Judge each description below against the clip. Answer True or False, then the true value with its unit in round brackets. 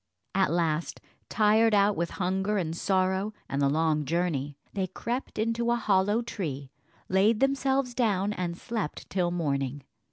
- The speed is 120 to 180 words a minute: True (150 wpm)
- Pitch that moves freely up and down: False (4.8 semitones)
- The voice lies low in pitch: False (190 Hz)